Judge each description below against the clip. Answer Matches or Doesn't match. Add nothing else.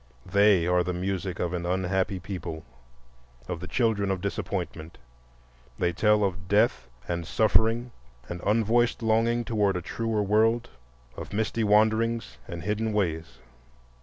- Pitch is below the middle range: Matches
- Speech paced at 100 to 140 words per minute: Matches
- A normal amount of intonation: Matches